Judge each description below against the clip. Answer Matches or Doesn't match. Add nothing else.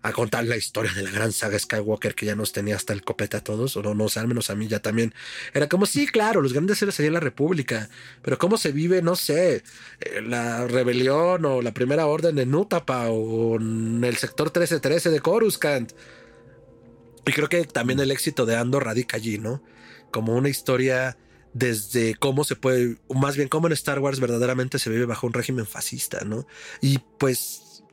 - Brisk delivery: Matches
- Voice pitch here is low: Matches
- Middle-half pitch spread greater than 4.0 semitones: Matches